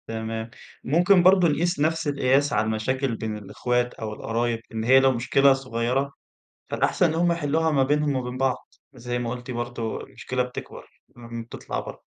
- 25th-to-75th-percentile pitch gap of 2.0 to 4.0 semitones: Yes, average, 3.6 semitones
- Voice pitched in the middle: No, low, 130 Hz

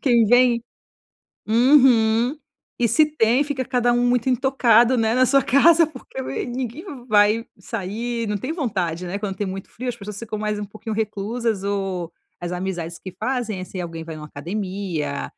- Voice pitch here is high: Yes, high, 225 Hz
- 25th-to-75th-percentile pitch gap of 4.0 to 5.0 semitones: Yes, average, 4.3 semitones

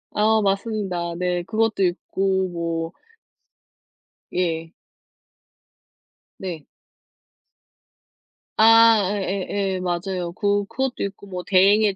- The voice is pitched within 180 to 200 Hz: Yes, high, 190 Hz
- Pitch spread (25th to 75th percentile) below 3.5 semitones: Yes, average, 2.8 semitones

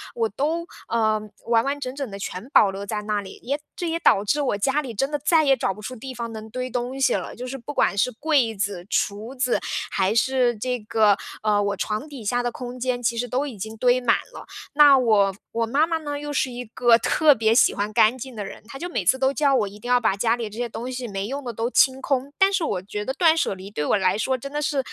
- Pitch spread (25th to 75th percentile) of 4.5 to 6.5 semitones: No, average, 4.1 semitones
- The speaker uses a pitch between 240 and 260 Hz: Yes, high, 245 Hz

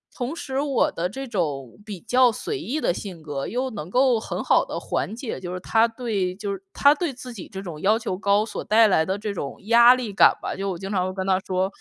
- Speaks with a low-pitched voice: No, high, 205 Hz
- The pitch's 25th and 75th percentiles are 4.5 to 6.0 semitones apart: Yes, average, 4.8 semitones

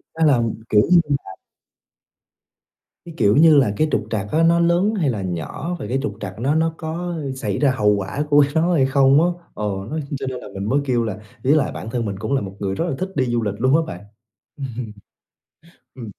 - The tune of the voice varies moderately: No, wide, 6.8 semitones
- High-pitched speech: No, low, 135 Hz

